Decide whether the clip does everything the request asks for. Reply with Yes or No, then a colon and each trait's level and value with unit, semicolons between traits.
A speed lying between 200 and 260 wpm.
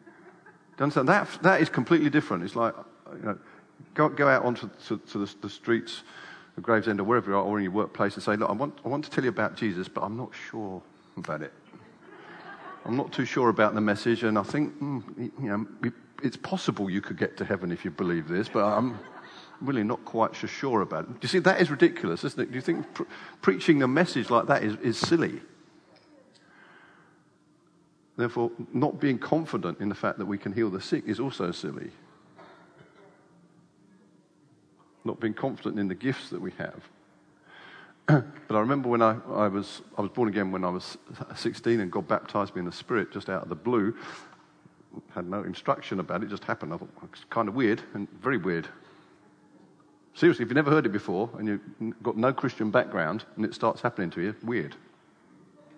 Yes: fast, 205 wpm